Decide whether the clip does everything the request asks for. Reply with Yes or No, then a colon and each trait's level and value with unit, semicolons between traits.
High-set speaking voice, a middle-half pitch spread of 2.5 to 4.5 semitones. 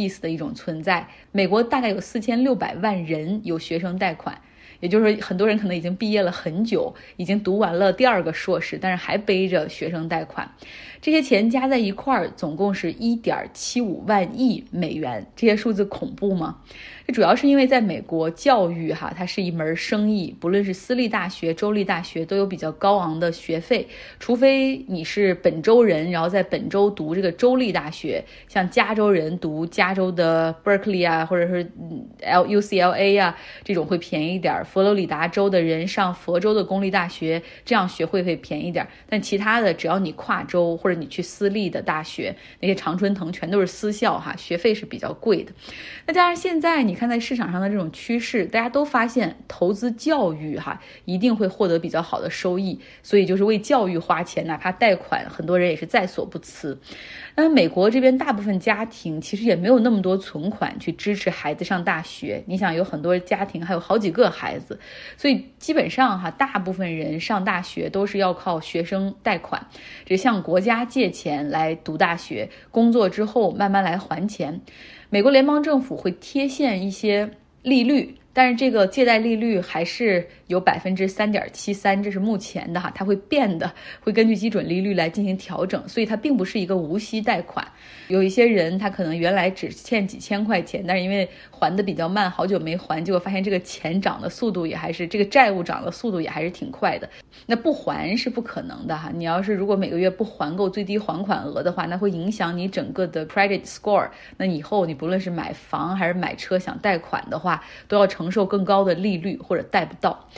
Yes: high, 195 Hz; average, 3.7 semitones